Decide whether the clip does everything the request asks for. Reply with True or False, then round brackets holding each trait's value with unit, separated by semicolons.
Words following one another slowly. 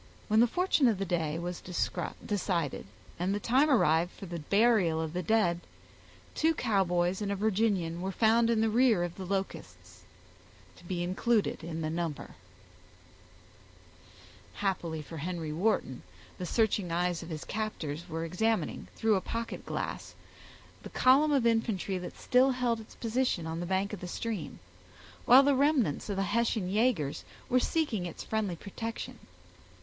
False (160 wpm)